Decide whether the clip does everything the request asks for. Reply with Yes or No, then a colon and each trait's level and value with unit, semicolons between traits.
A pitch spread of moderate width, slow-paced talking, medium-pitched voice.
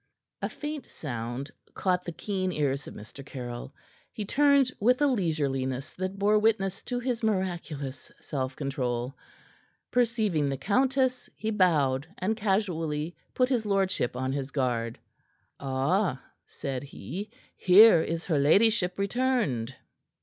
No: wide, 8.0 semitones; slow, 130 wpm; medium, 180 Hz